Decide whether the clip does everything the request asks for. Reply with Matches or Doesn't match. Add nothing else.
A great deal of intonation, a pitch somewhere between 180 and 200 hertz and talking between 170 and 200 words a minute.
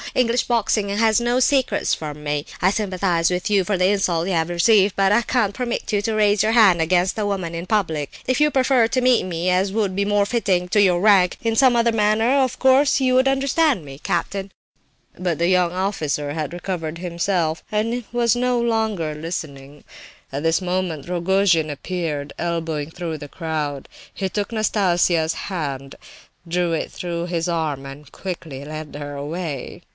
Doesn't match